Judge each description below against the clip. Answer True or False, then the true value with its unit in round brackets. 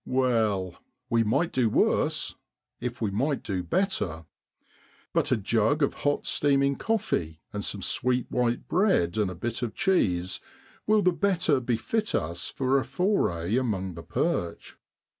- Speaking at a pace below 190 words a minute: True (150 wpm)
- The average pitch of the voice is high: False (120 Hz)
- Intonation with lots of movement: True (7.2 semitones)